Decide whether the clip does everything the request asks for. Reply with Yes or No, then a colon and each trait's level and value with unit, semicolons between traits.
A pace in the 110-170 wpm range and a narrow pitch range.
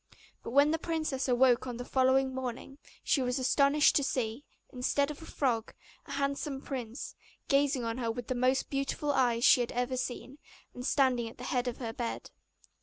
No: average, 190 wpm; narrow, 2.2 semitones